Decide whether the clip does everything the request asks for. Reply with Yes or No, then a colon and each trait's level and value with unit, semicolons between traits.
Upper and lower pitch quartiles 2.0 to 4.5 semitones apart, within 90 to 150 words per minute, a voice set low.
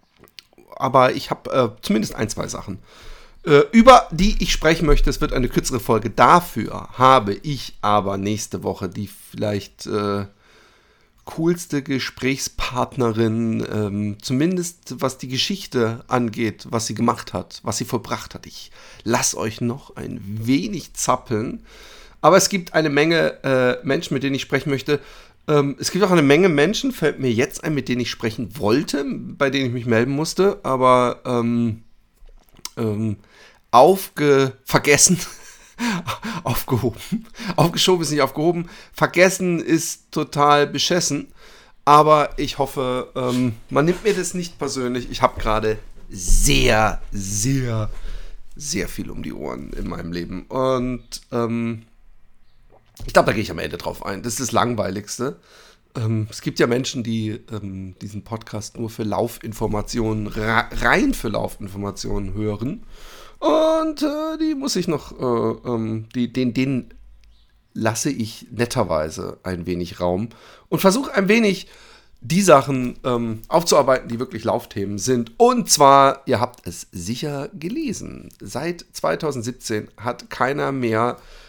No: average, 5.1 semitones; average, 145 wpm; low, 125 Hz